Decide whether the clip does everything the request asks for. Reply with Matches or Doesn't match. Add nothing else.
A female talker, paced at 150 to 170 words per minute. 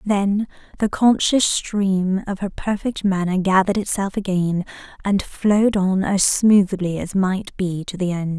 Matches